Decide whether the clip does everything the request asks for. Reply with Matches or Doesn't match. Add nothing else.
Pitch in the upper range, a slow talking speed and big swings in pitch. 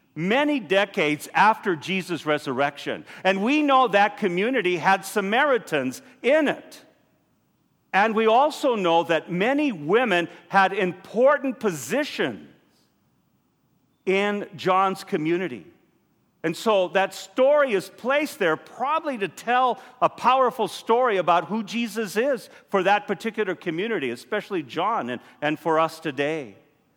Matches